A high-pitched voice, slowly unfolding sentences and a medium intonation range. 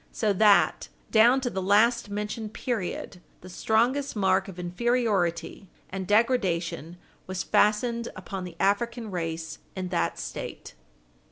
Yes: high, 200 Hz; slow, 125 wpm; average, 4.4 semitones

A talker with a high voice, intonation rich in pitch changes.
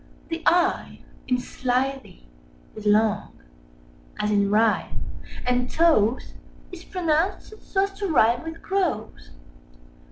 Yes: very high, 255 Hz; wide, 7.6 semitones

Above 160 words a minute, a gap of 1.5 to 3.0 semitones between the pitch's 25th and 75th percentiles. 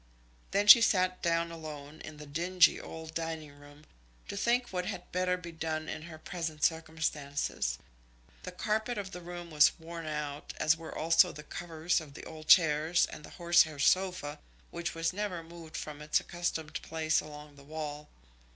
Yes: average, 175 wpm; narrow, 2.5 semitones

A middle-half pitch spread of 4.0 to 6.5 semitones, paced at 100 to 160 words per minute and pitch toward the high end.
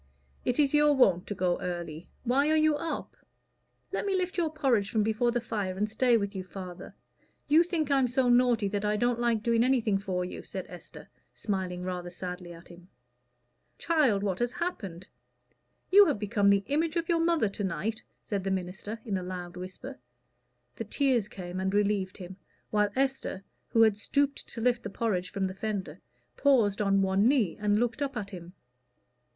No: wide, 5.4 semitones; average, 190 wpm; high, 210 Hz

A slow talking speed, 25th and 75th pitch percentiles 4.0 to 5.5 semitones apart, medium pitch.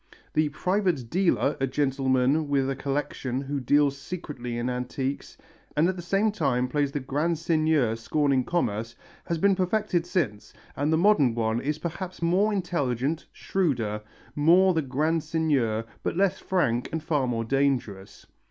No: average, 155 wpm; average, 5.0 semitones; medium, 145 Hz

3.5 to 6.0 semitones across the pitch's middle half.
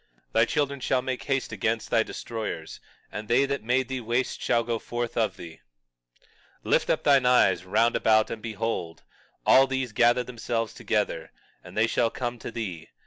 No: narrow, 2.4 semitones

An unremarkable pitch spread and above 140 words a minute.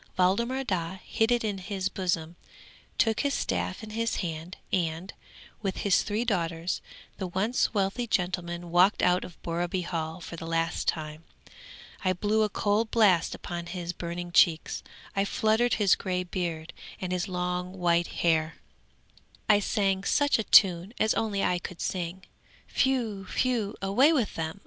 Yes: average, 3.5 semitones; average, 160 wpm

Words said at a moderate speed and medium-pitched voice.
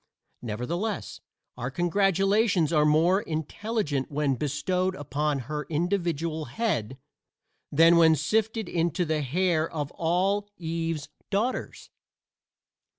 No: slow, 100 wpm; medium, 165 Hz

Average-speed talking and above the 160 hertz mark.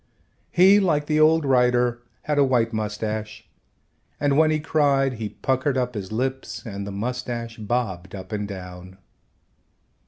No: average, 150 wpm; low, 125 Hz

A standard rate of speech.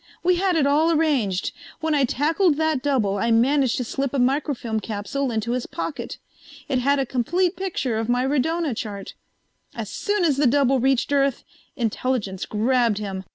Yes: average, 175 wpm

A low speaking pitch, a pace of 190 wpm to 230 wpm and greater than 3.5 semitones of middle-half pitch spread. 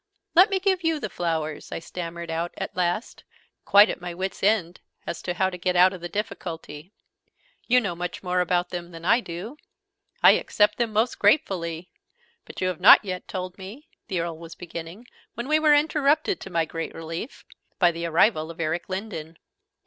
No: medium, 180 Hz; average, 195 wpm; average, 4.4 semitones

